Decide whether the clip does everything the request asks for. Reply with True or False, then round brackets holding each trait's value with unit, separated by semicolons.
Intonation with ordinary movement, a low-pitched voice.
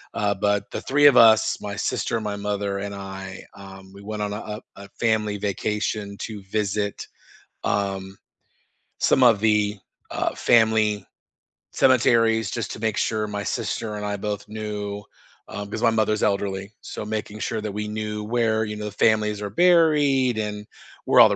False (1.4 semitones; 105 Hz)